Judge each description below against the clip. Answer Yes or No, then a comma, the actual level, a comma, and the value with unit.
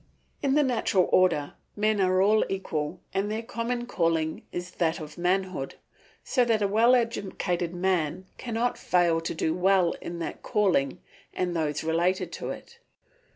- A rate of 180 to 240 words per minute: No, average, 155 wpm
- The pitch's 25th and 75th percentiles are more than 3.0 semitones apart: Yes, average, 4.4 semitones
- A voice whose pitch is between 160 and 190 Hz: Yes, medium, 185 Hz